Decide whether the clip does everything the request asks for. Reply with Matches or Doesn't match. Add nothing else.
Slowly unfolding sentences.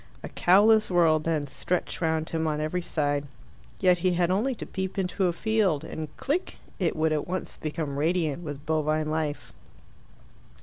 Doesn't match